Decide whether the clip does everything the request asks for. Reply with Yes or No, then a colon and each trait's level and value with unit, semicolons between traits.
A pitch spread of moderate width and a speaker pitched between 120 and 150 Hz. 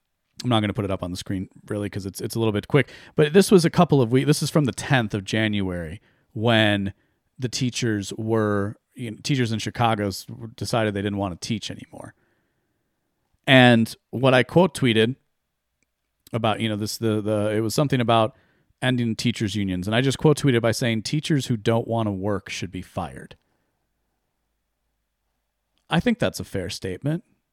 No: average, 3.9 semitones; low, 110 Hz